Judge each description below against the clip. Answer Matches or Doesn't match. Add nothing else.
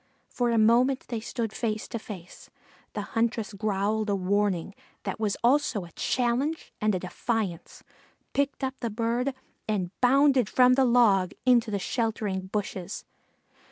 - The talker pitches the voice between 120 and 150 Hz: Doesn't match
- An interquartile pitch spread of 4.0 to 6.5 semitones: Doesn't match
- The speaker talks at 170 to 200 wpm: Doesn't match